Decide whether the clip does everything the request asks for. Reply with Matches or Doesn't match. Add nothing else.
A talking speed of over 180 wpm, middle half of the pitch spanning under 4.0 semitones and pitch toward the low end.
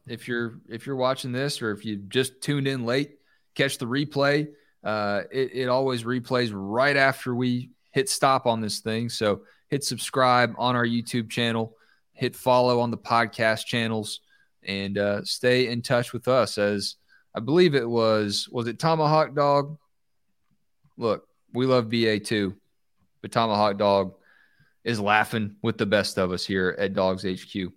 Doesn't match